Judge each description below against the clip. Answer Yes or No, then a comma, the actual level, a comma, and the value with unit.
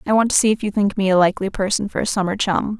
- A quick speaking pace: Yes, fast, 320 wpm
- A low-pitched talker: No, high, 200 Hz